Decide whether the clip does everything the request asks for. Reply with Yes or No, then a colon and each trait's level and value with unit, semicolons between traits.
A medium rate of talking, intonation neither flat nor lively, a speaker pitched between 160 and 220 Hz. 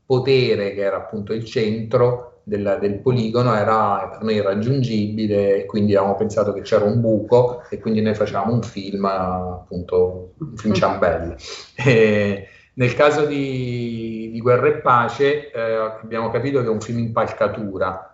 No: average, 155 wpm; average, 3.2 semitones; low, 110 Hz